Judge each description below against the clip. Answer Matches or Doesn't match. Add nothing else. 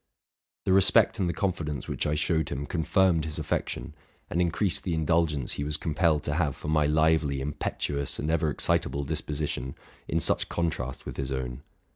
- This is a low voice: Matches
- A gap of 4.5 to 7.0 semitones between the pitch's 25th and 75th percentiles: Doesn't match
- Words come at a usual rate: Matches